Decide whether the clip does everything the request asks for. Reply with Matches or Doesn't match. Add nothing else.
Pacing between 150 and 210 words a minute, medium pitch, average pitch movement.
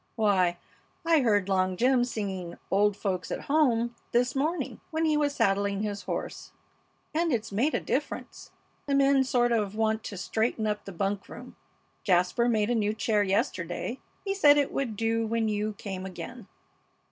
Doesn't match